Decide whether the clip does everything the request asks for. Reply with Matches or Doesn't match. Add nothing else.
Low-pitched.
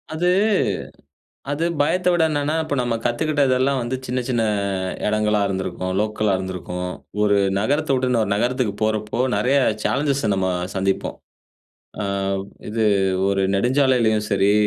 Matches